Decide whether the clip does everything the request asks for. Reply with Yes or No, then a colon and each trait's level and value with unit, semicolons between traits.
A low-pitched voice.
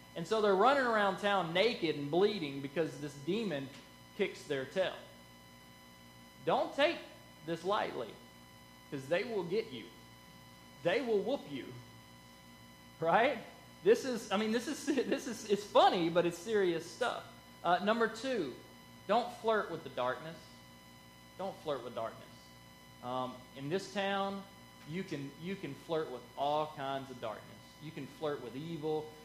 No: medium, 165 Hz